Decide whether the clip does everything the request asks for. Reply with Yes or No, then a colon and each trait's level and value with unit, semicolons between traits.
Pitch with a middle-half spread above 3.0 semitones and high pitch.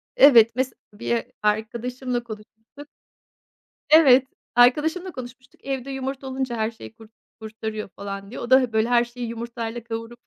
No: average, 2.7 semitones; high, 240 Hz